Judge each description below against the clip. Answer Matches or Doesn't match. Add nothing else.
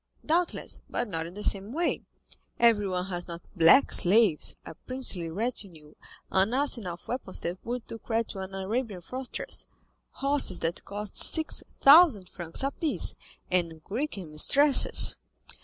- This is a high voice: Matches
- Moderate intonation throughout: Doesn't match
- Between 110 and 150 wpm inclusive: Matches